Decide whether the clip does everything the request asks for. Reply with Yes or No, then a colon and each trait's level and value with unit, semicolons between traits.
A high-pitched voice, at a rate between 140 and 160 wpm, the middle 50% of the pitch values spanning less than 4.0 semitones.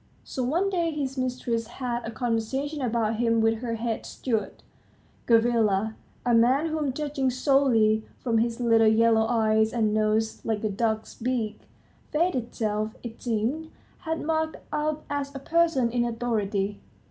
Yes: high, 235 Hz; average, 150 wpm; average, 3.6 semitones